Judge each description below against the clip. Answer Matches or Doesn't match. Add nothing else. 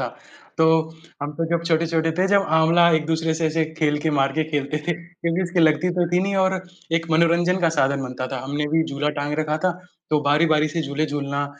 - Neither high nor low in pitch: Matches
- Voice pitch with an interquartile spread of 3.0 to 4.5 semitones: Doesn't match